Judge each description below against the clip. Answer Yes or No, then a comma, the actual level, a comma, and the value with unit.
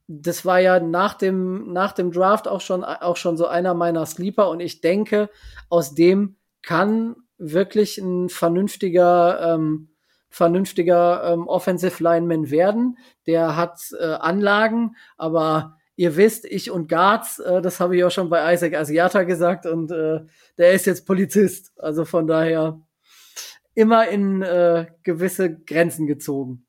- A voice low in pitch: No, medium, 175 Hz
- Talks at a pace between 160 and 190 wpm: No, average, 150 wpm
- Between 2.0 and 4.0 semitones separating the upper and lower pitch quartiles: Yes, narrow, 2.5 semitones